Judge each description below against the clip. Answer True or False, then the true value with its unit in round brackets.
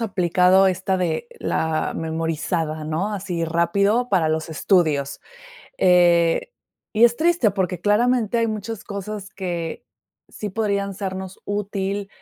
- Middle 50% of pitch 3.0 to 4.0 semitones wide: True (3.5 semitones)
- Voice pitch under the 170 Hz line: False (190 Hz)